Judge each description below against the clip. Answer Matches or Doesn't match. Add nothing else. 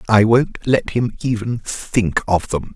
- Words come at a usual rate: Matches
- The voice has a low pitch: Matches